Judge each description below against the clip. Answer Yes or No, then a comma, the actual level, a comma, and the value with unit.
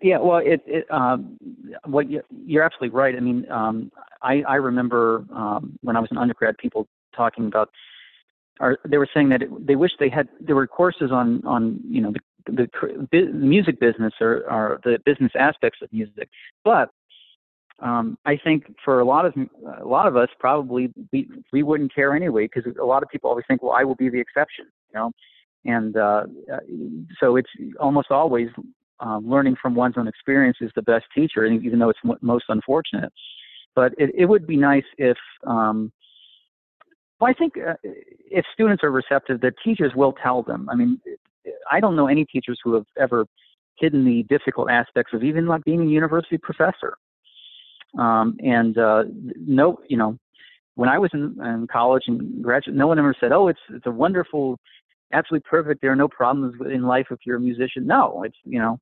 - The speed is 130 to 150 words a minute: No, average, 195 wpm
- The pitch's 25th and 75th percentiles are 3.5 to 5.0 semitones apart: No, wide, 5.4 semitones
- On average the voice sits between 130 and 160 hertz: Yes, low, 135 Hz